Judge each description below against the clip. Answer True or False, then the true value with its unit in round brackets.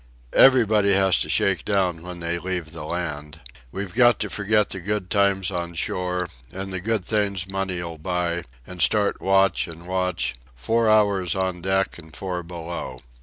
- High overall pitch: False (95 Hz)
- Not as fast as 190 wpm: True (170 wpm)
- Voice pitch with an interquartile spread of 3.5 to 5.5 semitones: False (2.4 semitones)